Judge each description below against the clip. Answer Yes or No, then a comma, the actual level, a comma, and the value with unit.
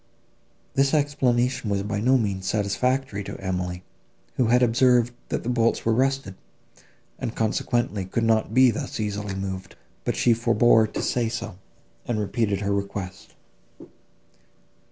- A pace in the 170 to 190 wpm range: No, average, 140 wpm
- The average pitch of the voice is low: Yes, low, 110 Hz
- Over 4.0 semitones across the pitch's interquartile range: No, average, 3.6 semitones